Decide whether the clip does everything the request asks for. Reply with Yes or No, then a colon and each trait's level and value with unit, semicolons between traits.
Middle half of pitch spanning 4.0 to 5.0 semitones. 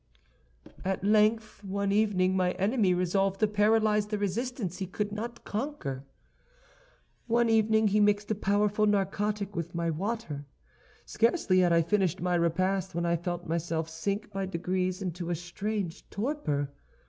No: average, 3.1 semitones